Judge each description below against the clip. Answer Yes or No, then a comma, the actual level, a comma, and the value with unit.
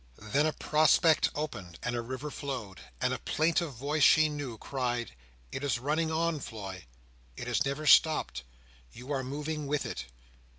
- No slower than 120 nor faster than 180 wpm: Yes, average, 165 wpm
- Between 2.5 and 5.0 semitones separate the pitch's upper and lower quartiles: Yes, average, 4.2 semitones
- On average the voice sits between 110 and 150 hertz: Yes, medium, 140 Hz